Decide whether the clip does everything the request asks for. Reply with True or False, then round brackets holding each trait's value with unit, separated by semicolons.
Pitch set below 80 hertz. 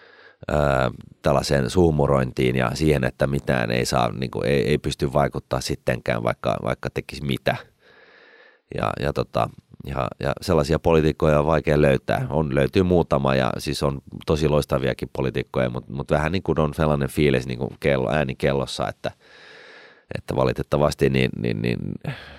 True (70 Hz)